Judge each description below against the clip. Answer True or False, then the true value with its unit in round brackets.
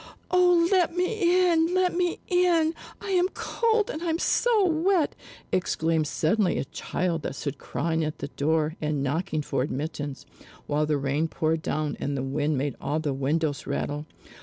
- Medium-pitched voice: True (160 Hz)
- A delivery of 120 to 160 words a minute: False (170 wpm)